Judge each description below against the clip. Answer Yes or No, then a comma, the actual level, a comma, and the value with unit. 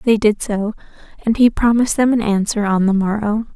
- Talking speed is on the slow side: No, fast, 205 wpm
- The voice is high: Yes, high, 215 Hz